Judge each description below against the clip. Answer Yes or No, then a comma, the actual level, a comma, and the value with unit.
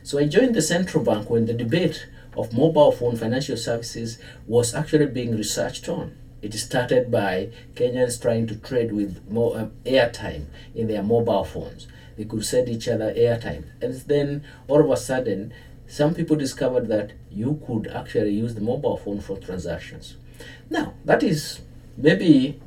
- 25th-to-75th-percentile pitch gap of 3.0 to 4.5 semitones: Yes, average, 4.0 semitones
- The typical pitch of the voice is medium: No, low, 120 Hz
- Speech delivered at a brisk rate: No, average, 165 wpm